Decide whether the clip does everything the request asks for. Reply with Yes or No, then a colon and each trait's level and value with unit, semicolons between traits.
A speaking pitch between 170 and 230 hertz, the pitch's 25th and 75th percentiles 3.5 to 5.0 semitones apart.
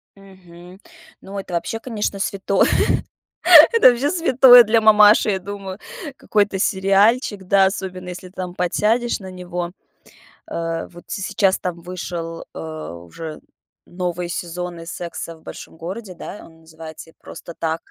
No: medium, 185 Hz; average, 3.0 semitones